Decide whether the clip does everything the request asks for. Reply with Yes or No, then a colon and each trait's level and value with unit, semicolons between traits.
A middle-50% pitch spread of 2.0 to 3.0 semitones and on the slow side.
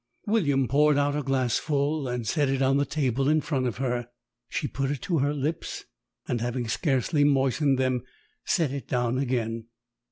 No: narrow, 2.6 semitones; average, 180 wpm